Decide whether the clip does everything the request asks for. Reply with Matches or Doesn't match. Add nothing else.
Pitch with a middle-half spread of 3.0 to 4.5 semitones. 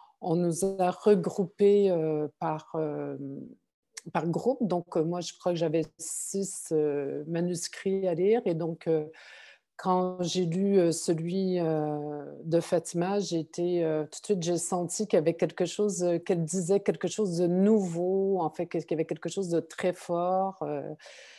Doesn't match